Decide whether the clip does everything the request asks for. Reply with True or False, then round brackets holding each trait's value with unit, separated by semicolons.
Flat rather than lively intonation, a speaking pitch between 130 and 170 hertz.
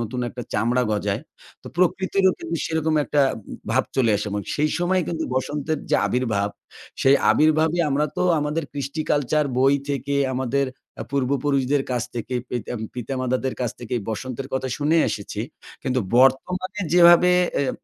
False (3.7 semitones; 135 Hz)